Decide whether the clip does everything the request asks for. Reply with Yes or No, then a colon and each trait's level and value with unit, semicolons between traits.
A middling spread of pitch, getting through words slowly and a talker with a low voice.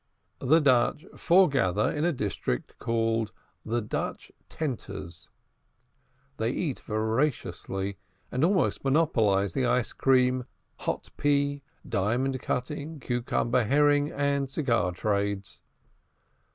Yes: average, 4.7 semitones; slow, 100 wpm; low, 125 Hz